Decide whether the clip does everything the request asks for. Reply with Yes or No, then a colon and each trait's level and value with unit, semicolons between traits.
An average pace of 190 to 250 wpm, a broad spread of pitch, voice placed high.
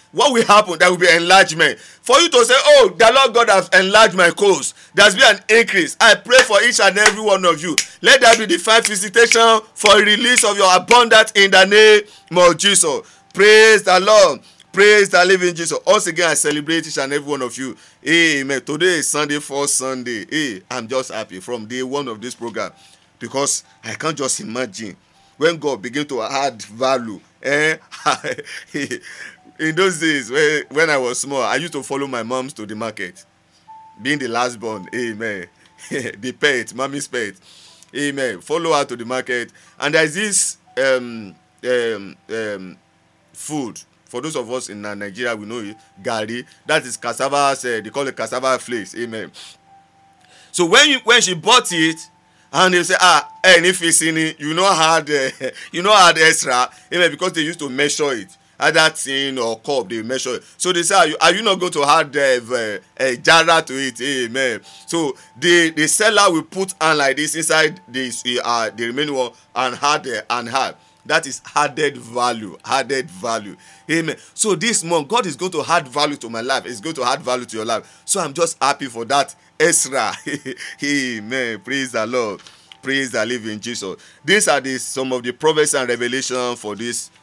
No: average, 195 wpm; wide, 6.3 semitones; medium, 145 Hz